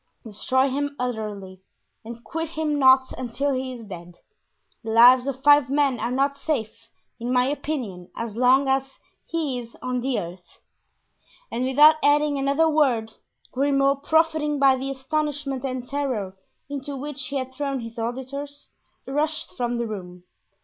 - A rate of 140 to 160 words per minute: Yes, average, 155 wpm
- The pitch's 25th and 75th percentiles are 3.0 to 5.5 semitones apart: Yes, average, 3.3 semitones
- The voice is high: Yes, very high, 265 Hz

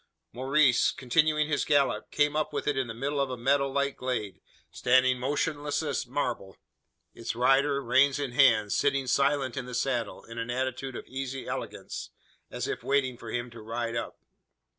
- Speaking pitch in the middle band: No, low, 130 Hz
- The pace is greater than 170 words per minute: Yes, average, 180 wpm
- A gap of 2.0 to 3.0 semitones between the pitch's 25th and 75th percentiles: Yes, narrow, 2.6 semitones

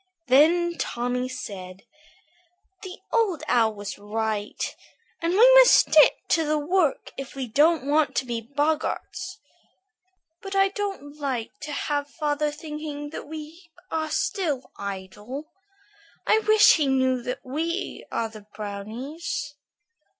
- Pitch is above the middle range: Yes, very high, 290 Hz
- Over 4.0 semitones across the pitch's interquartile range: Yes, wide, 5.4 semitones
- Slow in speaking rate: Yes, slow, 130 wpm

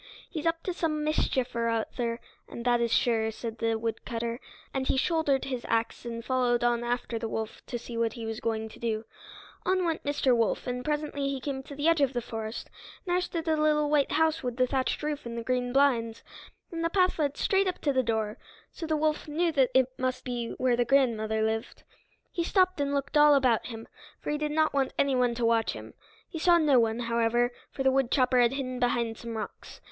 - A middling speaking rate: No, fast, 220 wpm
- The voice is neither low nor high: No, very high, 255 Hz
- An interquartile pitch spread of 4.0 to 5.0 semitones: Yes, average, 4.3 semitones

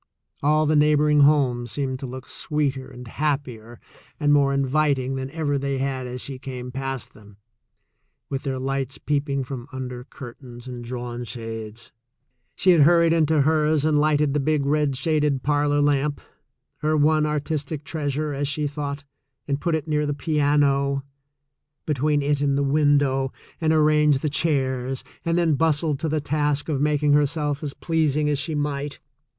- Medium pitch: Yes, medium, 145 Hz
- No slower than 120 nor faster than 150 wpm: No, average, 165 wpm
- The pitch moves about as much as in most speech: No, narrow, 2.1 semitones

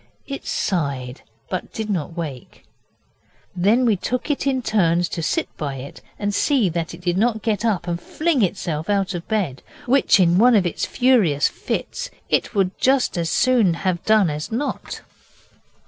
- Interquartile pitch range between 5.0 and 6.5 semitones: Yes, wide, 5.5 semitones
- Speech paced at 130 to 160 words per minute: No, average, 175 wpm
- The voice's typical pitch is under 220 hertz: Yes, high, 190 Hz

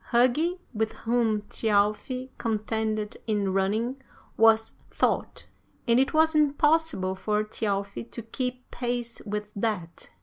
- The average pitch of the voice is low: No, high, 225 Hz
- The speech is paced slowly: Yes, slow, 115 wpm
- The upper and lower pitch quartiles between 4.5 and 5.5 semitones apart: No, average, 3.2 semitones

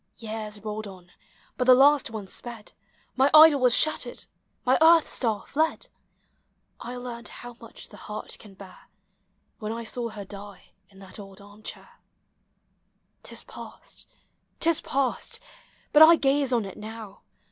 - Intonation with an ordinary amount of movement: Yes, average, 4.3 semitones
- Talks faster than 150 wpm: Yes, average, 160 wpm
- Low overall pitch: No, high, 230 Hz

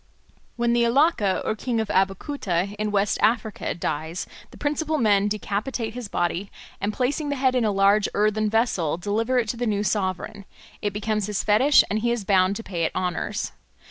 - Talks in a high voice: Yes, high, 210 Hz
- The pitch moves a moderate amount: Yes, average, 3.2 semitones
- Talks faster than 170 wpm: Yes, average, 190 wpm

